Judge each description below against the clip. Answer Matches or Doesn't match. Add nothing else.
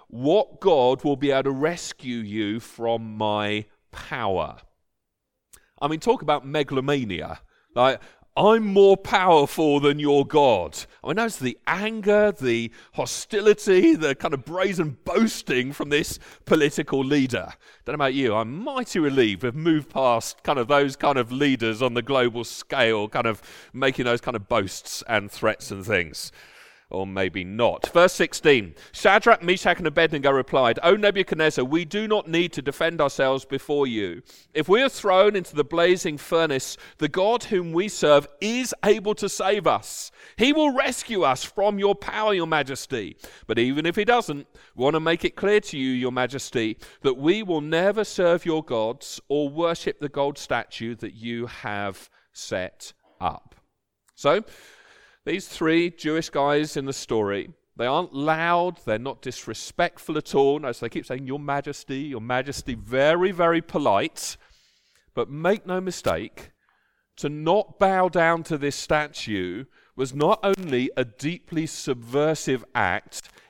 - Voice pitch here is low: Doesn't match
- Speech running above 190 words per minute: Doesn't match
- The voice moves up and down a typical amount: Doesn't match